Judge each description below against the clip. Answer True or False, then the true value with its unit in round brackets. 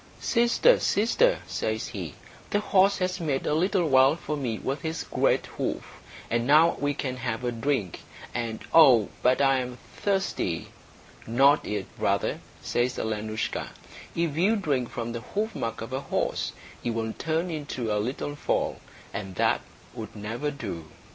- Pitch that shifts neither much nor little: False (6.1 semitones)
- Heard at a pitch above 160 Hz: False (135 Hz)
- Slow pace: False (160 wpm)